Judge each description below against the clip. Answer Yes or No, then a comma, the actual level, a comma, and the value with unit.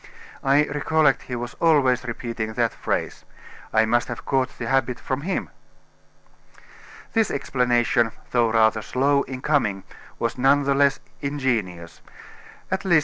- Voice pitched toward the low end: Yes, low, 130 Hz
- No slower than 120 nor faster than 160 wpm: Yes, average, 145 wpm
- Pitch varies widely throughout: No, average, 3.4 semitones